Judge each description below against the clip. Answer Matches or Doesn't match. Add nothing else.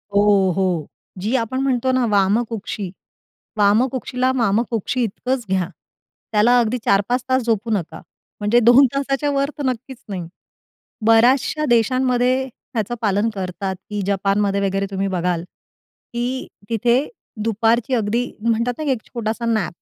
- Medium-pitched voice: Doesn't match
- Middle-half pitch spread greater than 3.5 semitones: Matches